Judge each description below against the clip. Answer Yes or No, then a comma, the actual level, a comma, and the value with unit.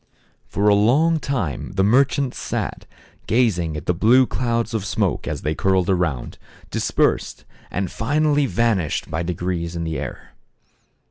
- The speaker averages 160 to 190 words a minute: No, average, 145 wpm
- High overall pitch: No, low, 100 Hz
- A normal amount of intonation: No, wide, 6.1 semitones